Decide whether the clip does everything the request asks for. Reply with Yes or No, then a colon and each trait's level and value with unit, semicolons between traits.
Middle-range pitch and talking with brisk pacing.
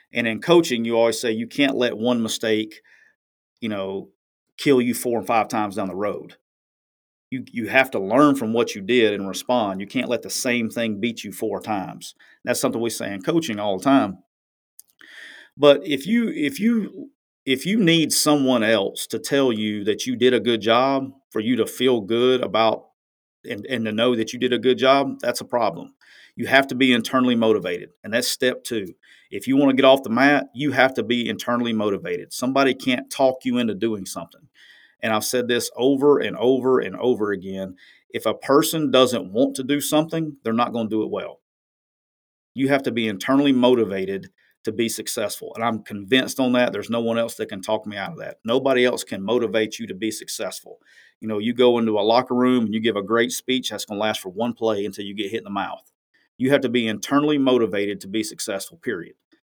No: low, 120 Hz; fast, 220 wpm